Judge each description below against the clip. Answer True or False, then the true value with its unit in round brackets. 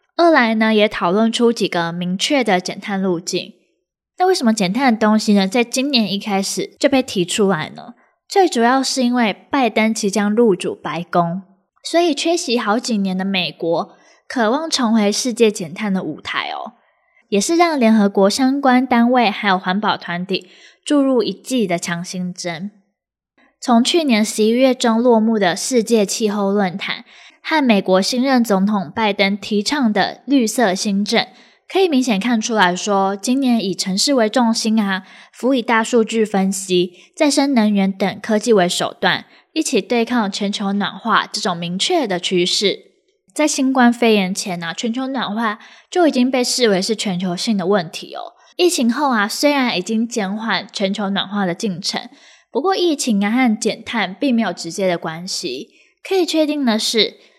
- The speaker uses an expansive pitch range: False (4.9 semitones)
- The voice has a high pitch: True (220 Hz)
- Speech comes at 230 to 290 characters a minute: True (255 characters per minute)